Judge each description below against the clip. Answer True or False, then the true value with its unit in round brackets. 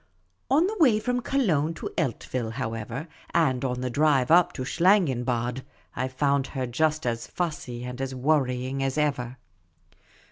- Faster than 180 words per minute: False (150 wpm)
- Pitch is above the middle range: False (135 Hz)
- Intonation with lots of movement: False (4.3 semitones)